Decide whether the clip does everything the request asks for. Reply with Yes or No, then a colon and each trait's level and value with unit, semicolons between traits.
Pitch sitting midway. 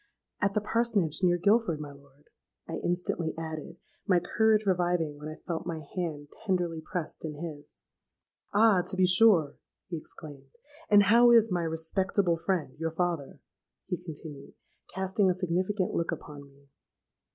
Yes: medium, 175 Hz